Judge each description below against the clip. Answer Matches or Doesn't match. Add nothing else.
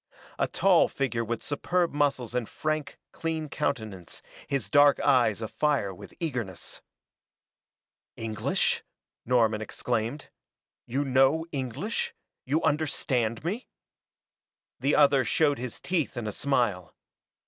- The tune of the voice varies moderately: Matches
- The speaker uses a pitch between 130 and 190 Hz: Matches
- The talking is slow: Matches